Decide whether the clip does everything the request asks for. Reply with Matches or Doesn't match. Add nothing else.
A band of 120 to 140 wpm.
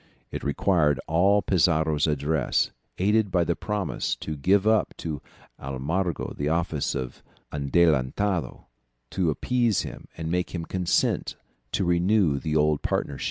Matches